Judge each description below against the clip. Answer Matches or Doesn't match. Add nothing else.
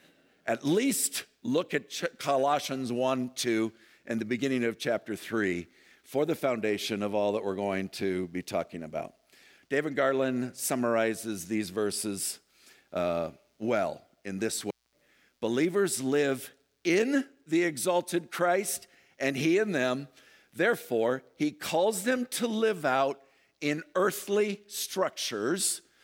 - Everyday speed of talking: Doesn't match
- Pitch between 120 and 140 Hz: Matches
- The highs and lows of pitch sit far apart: Matches